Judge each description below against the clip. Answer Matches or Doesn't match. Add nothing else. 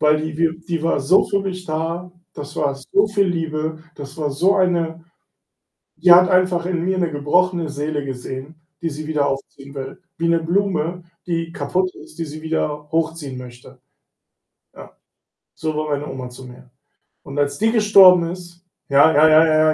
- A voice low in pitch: Doesn't match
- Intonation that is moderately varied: Matches